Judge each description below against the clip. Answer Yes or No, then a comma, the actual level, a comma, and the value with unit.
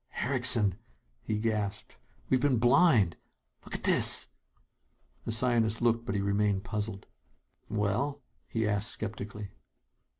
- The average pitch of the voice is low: Yes, low, 110 Hz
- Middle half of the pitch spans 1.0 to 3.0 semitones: Yes, average, 2.7 semitones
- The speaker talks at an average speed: No, slow, 125 wpm